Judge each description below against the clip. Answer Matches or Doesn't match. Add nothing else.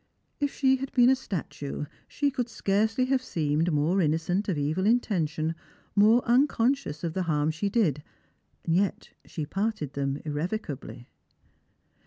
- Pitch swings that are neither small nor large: Doesn't match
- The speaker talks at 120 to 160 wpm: Matches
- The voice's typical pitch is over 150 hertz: Matches